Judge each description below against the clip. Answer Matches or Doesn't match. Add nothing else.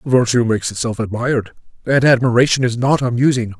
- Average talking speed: Matches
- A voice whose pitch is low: Matches